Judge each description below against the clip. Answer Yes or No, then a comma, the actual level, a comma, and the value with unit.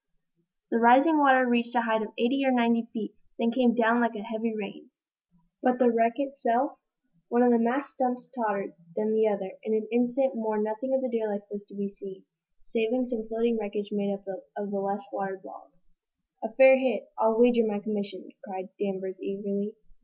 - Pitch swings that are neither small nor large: Yes, average, 3.2 semitones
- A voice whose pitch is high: Yes, high, 225 Hz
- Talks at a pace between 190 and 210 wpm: Yes, average, 195 wpm